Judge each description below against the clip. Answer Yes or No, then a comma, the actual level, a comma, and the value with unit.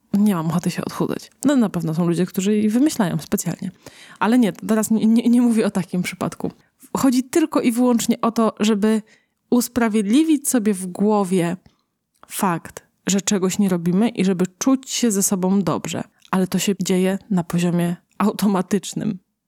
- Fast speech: Yes, fast, 165 wpm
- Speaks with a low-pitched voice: No, high, 205 Hz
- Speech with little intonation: No, average, 3.7 semitones